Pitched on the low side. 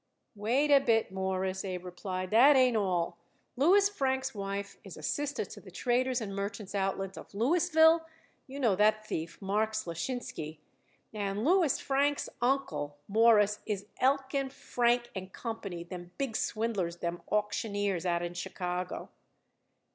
No: high, 210 Hz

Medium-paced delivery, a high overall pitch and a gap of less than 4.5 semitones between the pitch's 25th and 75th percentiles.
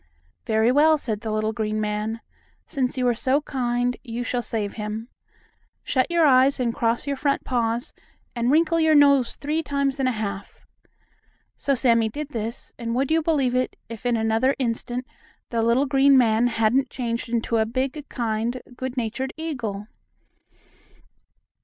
Yes: average, 160 wpm; high, 245 Hz; average, 3.3 semitones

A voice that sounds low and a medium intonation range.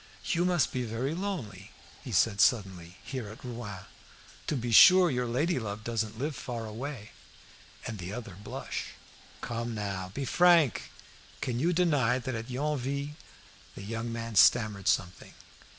Yes: low, 120 Hz; average, 5.0 semitones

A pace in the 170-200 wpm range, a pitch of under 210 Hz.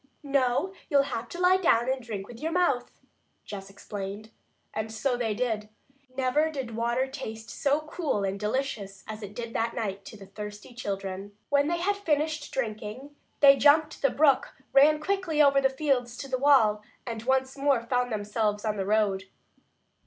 No: average, 175 wpm; high, 245 Hz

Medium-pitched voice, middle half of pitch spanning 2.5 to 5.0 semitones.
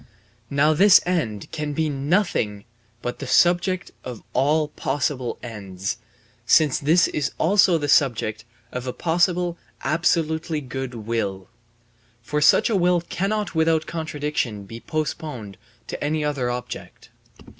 No: medium, 150 Hz; wide, 5.4 semitones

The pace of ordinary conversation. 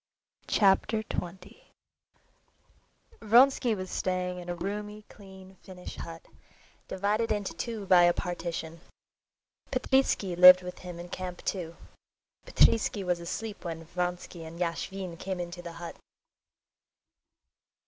No: slow, 115 wpm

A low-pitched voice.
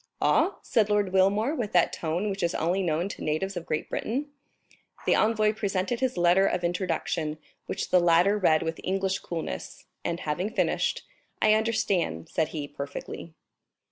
No: medium, 185 Hz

